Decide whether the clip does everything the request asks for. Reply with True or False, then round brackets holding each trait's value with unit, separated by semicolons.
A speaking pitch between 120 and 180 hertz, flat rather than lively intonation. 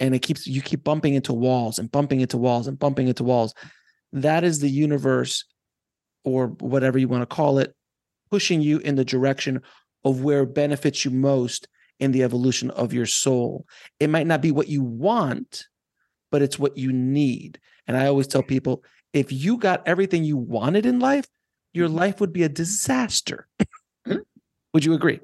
False (140 Hz; 3.3 semitones)